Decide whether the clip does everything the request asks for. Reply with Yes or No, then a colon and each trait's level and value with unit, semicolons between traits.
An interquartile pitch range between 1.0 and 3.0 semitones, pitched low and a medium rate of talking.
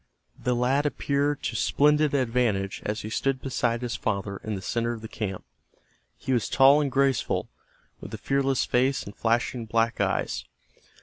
No: average, 3.4 semitones; low, 125 Hz; average, 170 wpm